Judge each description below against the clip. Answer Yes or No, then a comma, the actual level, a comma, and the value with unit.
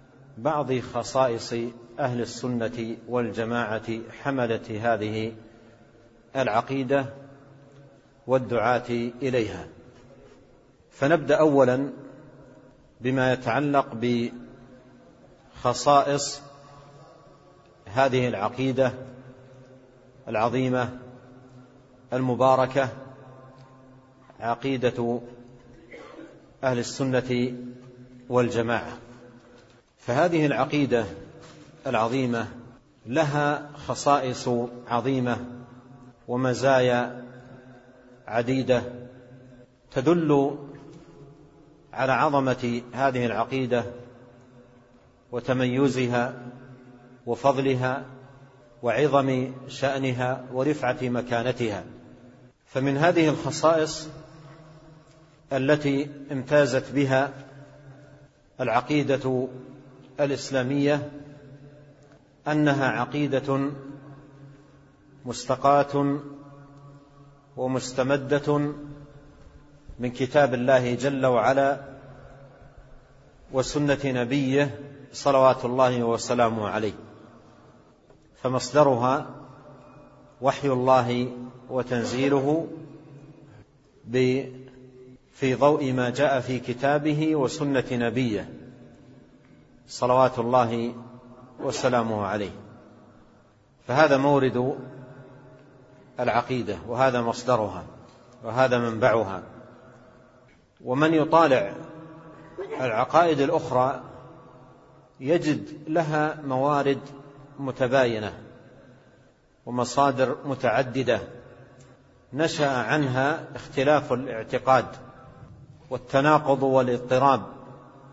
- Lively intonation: No, narrow, 2.4 semitones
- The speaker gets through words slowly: Yes, slow, 55 wpm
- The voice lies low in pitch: Yes, low, 130 Hz